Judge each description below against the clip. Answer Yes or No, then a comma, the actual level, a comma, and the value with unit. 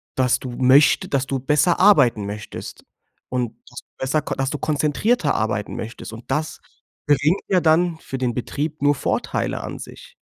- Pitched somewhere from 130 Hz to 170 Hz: Yes, medium, 140 Hz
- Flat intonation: No, average, 3.8 semitones